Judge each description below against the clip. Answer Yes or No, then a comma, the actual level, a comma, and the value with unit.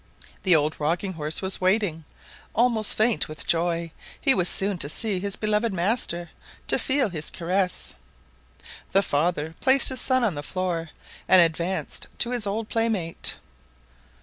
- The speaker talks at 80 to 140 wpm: No, average, 150 wpm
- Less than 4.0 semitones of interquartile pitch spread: No, average, 4.6 semitones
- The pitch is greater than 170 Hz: Yes, medium, 185 Hz